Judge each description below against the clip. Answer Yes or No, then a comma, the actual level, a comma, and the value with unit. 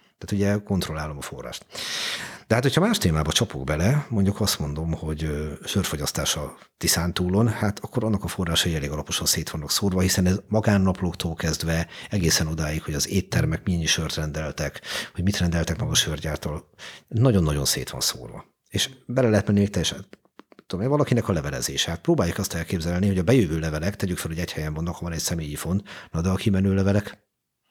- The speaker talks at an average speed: No, fast, 190 wpm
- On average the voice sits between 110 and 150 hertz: No, very low, 85 Hz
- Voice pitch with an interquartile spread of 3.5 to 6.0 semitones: Yes, average, 4.2 semitones